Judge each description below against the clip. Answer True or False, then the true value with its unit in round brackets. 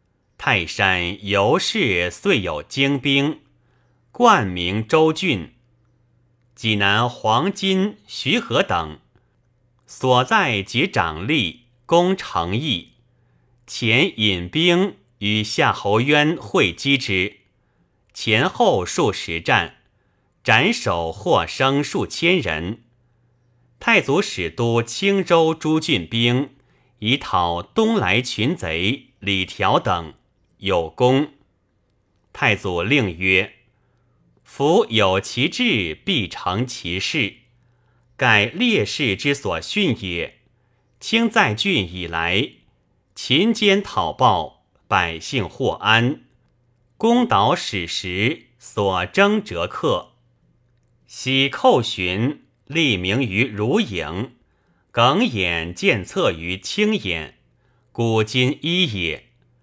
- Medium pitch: False (120 Hz)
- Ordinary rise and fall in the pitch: False (5.9 semitones)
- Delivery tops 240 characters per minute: False (130 characters per minute)